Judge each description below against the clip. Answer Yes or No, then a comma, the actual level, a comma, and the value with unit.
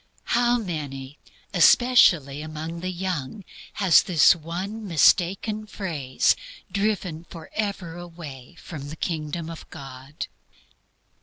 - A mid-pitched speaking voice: Yes, medium, 170 Hz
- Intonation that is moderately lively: Yes, average, 4.3 semitones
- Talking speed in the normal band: No, slow, 100 wpm